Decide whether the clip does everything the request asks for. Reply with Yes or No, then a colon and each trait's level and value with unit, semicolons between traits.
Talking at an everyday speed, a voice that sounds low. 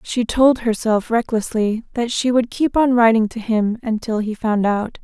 No: average, 190 wpm; high, 230 Hz